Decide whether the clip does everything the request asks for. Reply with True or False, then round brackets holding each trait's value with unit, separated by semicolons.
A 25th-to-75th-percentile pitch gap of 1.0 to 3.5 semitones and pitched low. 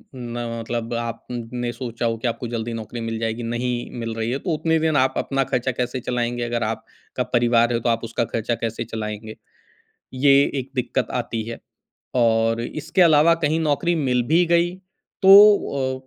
True (2.9 semitones; 120 Hz)